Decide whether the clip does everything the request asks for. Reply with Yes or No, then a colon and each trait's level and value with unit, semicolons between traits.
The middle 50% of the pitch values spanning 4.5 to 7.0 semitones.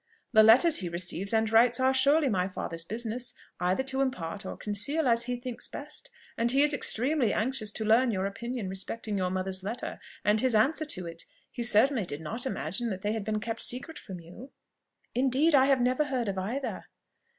Yes: average, 4.8 semitones